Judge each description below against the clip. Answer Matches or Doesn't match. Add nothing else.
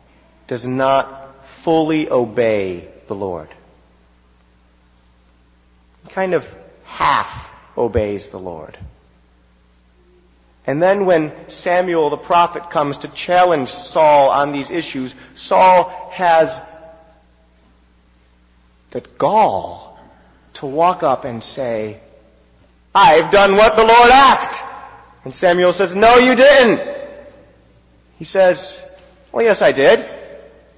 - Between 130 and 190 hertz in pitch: Matches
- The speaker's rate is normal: Doesn't match